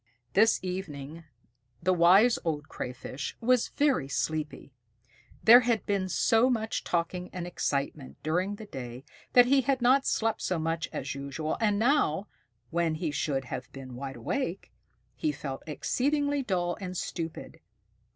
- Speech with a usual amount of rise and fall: No, wide, 7.3 semitones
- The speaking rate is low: No, average, 145 wpm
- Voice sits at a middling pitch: Yes, medium, 175 Hz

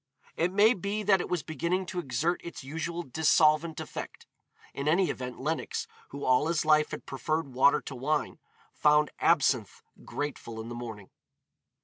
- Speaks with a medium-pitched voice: Yes, medium, 155 Hz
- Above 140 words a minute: Yes, average, 160 wpm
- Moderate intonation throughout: Yes, average, 4.2 semitones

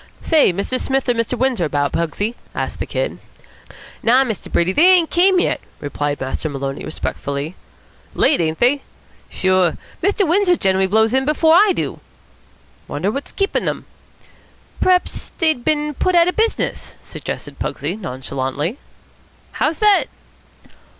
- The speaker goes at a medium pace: Yes, average, 145 wpm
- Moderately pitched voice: No, high, 245 Hz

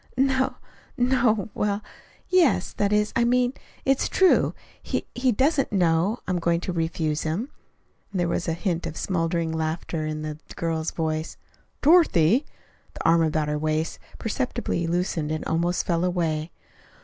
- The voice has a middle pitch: Yes, medium, 175 Hz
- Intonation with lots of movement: Yes, wide, 6.5 semitones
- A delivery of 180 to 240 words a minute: No, average, 155 wpm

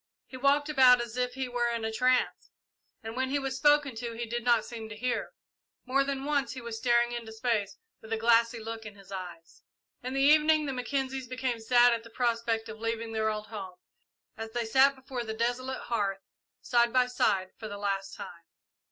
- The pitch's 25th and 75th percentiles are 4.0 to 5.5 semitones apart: No, average, 2.7 semitones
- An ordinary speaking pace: No, fast, 215 wpm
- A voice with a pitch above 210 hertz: Yes, high, 235 Hz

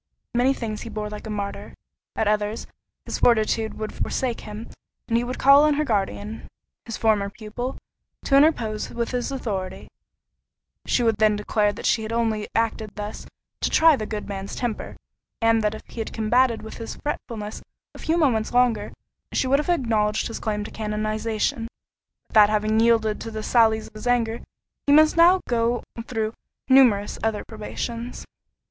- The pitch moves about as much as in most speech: No, narrow, 2.3 semitones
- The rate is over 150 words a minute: Yes, average, 175 wpm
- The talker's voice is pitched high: Yes, high, 225 Hz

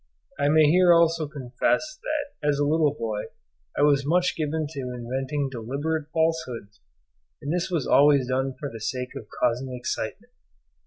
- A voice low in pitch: No, medium, 145 Hz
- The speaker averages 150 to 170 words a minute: Yes, average, 160 wpm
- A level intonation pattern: No, average, 3.9 semitones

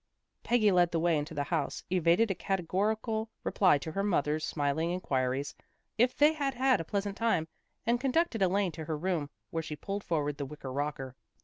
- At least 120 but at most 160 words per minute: No, average, 190 wpm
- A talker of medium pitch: Yes, medium, 175 Hz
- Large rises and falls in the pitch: Yes, wide, 6.1 semitones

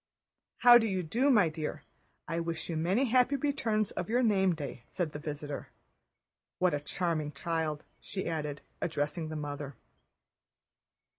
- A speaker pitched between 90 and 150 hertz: No, medium, 165 Hz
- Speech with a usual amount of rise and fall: No, wide, 5.9 semitones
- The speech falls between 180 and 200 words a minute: No, average, 150 wpm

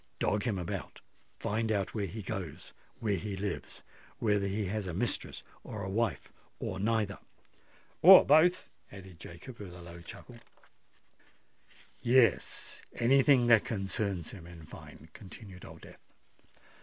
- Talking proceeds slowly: Yes, slow, 130 wpm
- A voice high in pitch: No, low, 100 Hz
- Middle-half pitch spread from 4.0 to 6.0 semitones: No, average, 3.5 semitones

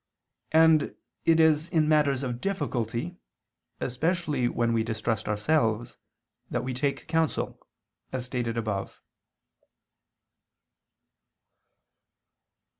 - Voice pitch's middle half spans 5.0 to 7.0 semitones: Yes, average, 5.3 semitones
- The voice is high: No, low, 130 Hz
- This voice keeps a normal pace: No, slow, 90 wpm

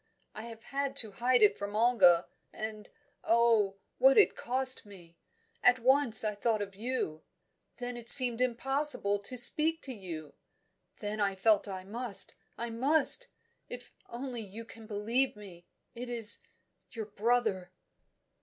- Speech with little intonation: No, average, 3.4 semitones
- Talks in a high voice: Yes, high, 230 Hz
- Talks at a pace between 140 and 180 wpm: Yes, average, 145 wpm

